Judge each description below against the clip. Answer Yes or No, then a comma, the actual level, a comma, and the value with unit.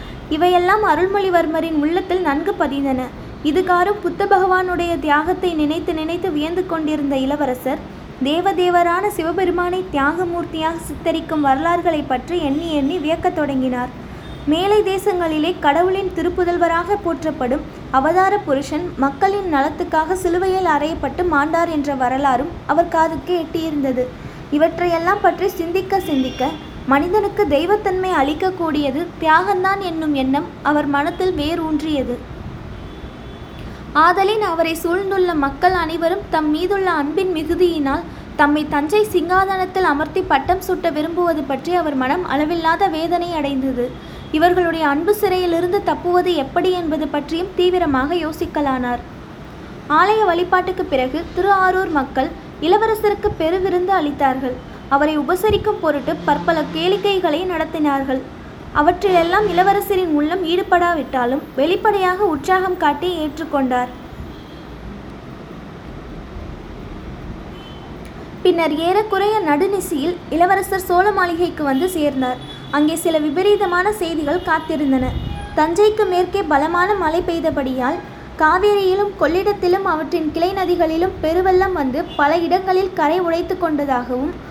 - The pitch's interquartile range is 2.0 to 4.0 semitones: Yes, average, 3.6 semitones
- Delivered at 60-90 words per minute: No, average, 100 wpm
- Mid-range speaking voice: No, very high, 335 Hz